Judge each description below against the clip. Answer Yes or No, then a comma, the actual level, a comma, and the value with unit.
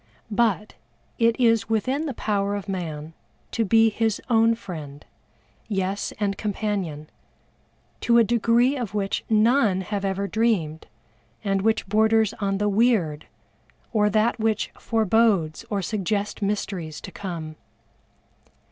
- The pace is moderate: No, slow, 130 wpm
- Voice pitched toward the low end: No, high, 210 Hz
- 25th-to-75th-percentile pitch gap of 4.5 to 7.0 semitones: No, average, 2.8 semitones